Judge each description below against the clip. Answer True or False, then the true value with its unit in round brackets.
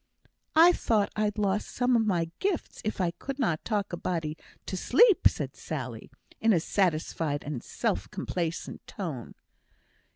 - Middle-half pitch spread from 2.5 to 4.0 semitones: False (5.4 semitones)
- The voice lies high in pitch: True (195 Hz)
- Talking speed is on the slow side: False (155 wpm)